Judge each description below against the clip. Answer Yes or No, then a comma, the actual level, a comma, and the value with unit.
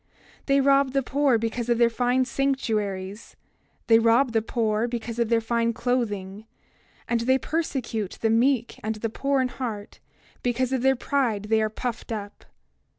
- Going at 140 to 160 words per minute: No, average, 170 wpm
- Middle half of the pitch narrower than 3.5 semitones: Yes, average, 2.8 semitones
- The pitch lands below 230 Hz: No, high, 235 Hz